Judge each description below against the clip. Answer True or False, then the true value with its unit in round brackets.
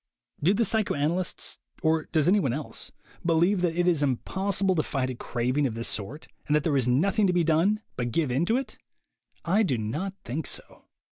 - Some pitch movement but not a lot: False (5.7 semitones)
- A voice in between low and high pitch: True (160 Hz)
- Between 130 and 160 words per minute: False (200 wpm)